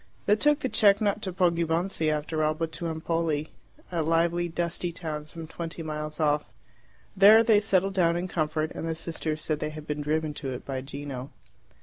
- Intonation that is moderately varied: No, narrow, 2.3 semitones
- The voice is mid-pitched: Yes, medium, 165 Hz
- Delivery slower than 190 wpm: No, average, 195 wpm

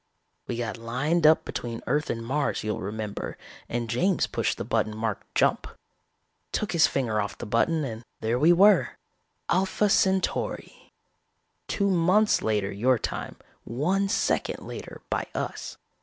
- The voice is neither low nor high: No, low, 125 Hz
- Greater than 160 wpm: No, average, 145 wpm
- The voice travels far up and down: Yes, wide, 7.8 semitones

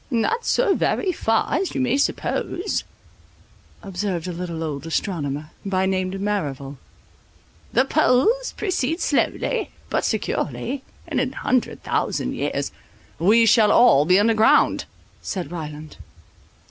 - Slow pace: Yes, slow, 120 wpm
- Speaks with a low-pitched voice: No, high, 205 Hz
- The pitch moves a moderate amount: No, wide, 7.4 semitones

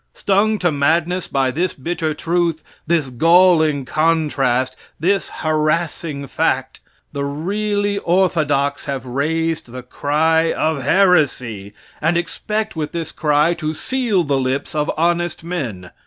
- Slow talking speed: Yes, slow, 125 wpm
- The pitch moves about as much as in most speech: Yes, average, 3.6 semitones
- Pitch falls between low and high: Yes, medium, 160 Hz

